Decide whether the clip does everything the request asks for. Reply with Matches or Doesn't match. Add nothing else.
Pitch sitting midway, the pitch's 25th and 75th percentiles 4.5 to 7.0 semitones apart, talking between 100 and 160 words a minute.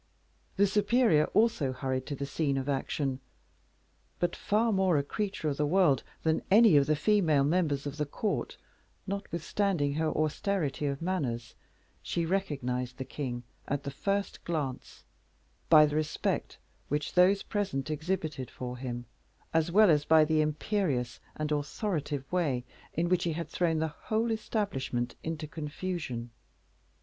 Matches